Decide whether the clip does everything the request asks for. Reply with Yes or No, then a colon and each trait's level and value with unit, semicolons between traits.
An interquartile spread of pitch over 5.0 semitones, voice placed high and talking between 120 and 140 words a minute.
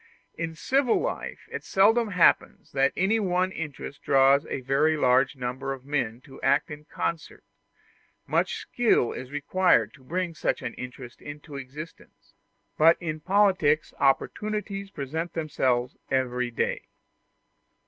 No: wide, 5.6 semitones; medium, 150 Hz; slow, 135 wpm